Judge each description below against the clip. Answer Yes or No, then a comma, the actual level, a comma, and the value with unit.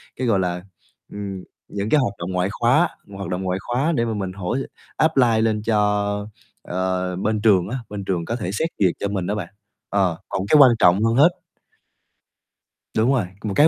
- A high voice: No, low, 100 Hz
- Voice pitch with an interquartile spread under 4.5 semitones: Yes, average, 4.1 semitones